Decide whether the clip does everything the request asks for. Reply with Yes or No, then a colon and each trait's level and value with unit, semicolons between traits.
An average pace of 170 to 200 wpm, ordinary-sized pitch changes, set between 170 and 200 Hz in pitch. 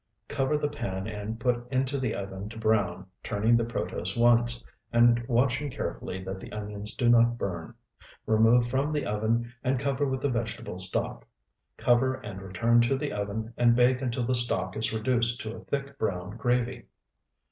No: average, 175 wpm; average, 3.0 semitones; low, 120 Hz